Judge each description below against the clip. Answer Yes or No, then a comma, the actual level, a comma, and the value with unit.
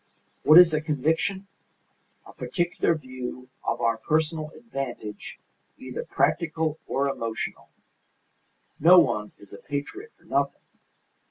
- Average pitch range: Yes, average, 4.8 semitones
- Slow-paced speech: Yes, slow, 115 wpm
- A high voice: No, medium, 155 Hz